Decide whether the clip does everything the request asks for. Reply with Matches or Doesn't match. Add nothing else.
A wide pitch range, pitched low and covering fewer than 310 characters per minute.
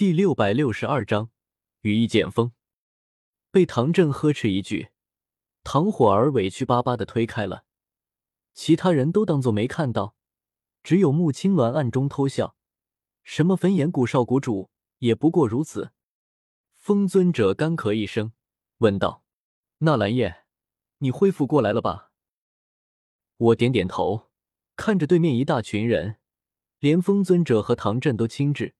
Matches